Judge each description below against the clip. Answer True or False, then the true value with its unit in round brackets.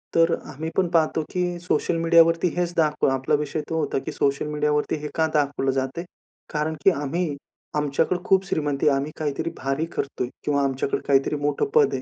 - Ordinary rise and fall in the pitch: True (3.0 semitones)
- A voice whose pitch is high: False (150 Hz)